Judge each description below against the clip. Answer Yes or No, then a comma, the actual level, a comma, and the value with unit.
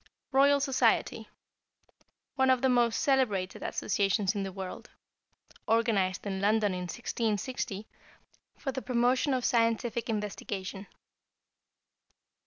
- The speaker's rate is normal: No, slow, 105 wpm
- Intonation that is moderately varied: Yes, average, 4.3 semitones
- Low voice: No, high, 225 Hz